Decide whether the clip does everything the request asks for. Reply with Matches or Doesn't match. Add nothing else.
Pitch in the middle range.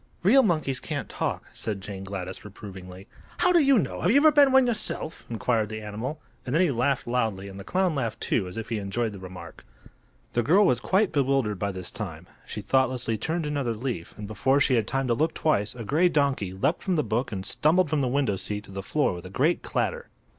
Doesn't match